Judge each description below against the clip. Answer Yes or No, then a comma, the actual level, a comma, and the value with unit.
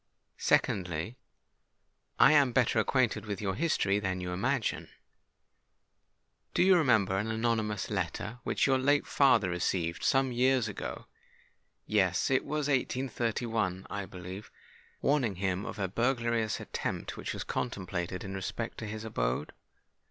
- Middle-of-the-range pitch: No, low, 110 Hz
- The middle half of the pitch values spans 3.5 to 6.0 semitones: Yes, average, 5.1 semitones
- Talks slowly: Yes, slow, 125 wpm